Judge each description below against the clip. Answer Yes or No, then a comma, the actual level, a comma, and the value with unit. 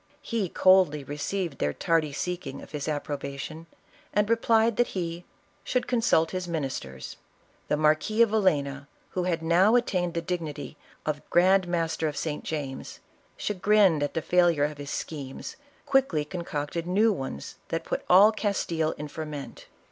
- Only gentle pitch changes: No, average, 4.3 semitones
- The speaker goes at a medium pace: Yes, average, 160 wpm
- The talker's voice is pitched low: No, medium, 165 Hz